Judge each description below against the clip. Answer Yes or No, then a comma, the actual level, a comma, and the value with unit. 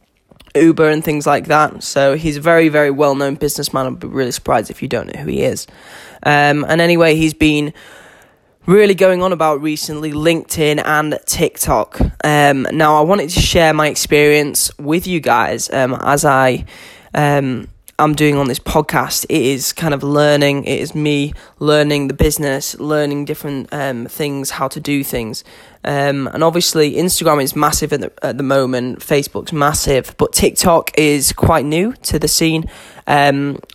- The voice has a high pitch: No, medium, 150 Hz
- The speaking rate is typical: Yes, average, 175 wpm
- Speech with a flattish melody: Yes, narrow, 1.7 semitones